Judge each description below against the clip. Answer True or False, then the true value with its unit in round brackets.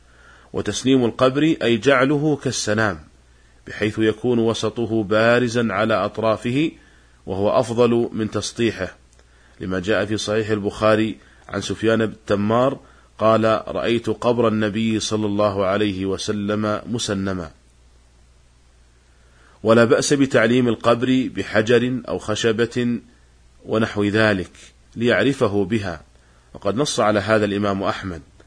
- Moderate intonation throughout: True (4.0 semitones)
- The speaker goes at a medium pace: True (105 wpm)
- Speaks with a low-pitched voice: True (105 Hz)